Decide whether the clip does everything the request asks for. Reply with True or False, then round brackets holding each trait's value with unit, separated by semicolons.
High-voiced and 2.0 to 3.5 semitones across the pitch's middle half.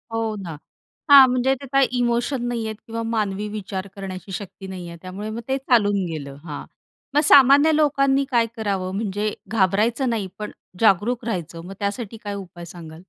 False (210 Hz; 4.2 semitones)